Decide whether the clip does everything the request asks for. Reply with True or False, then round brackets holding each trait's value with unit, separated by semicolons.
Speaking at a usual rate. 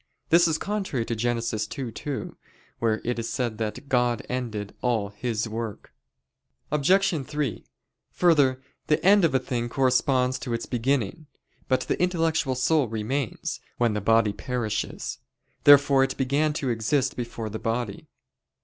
True (145 wpm)